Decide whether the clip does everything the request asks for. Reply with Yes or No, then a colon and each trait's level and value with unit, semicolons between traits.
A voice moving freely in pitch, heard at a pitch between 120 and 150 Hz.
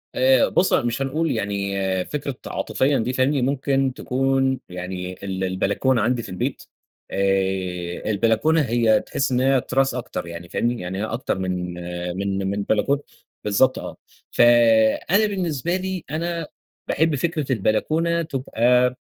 Yes: wide, 5.8 semitones; low, 125 Hz